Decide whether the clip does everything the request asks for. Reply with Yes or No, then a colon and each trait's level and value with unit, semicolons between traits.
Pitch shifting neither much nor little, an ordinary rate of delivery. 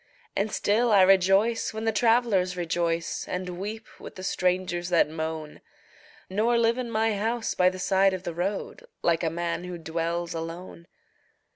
Yes: average, 4.0 semitones; average, 165 wpm